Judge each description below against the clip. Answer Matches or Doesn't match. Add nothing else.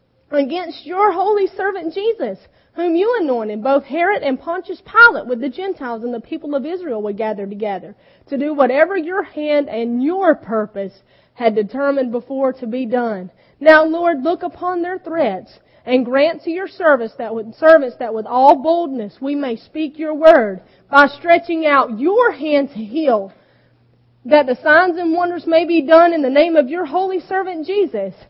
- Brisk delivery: Doesn't match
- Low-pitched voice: Doesn't match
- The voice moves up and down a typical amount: Doesn't match